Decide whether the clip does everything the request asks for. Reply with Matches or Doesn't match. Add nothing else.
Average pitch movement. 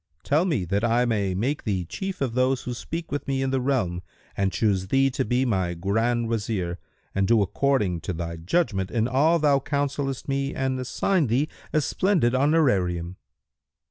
Doesn't match